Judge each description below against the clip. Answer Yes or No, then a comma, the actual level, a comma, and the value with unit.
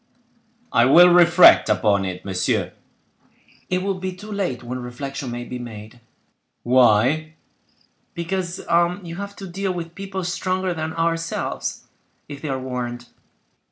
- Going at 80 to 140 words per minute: Yes, slow, 135 wpm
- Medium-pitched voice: Yes, medium, 160 Hz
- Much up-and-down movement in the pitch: Yes, wide, 6.9 semitones